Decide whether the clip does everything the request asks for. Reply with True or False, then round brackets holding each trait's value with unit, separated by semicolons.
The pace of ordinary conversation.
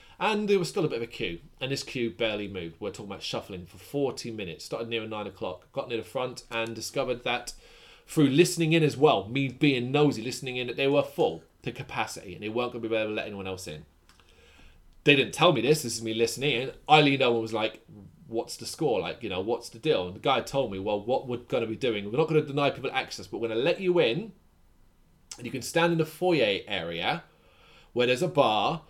False (255 wpm)